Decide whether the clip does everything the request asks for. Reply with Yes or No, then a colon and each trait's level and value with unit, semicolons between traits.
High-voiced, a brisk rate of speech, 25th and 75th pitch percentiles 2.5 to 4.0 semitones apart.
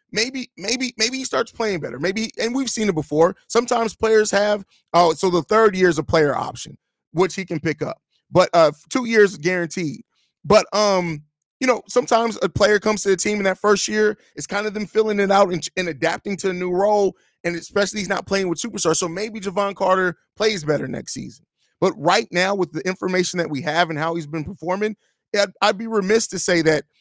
Yes: high, 195 Hz; fast, 225 wpm; average, 3.6 semitones